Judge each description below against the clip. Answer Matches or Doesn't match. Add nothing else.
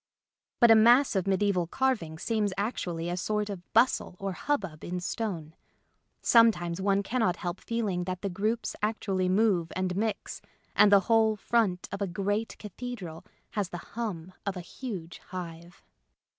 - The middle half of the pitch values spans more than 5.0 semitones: Doesn't match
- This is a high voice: Matches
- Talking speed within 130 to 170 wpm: Matches